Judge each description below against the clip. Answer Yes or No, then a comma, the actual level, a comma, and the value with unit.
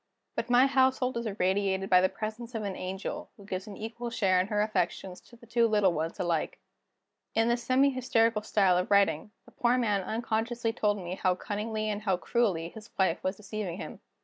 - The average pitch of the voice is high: Yes, high, 210 Hz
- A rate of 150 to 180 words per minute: No, average, 200 wpm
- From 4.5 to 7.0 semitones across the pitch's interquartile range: No, average, 3.6 semitones